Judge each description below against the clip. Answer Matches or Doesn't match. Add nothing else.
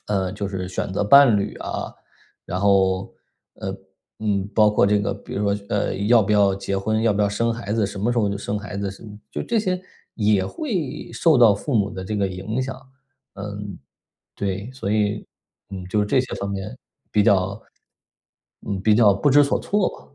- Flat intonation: Matches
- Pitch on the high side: Doesn't match